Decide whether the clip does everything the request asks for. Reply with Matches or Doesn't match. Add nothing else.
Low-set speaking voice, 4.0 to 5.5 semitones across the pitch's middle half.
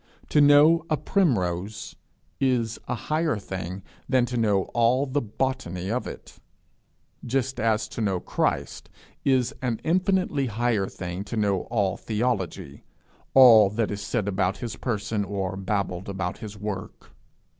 Matches